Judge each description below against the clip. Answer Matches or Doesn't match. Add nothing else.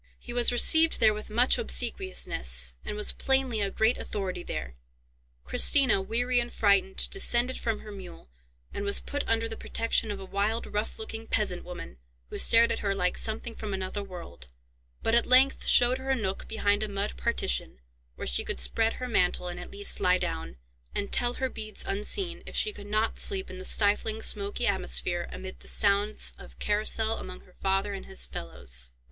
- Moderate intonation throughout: Matches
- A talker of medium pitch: Doesn't match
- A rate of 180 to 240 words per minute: Matches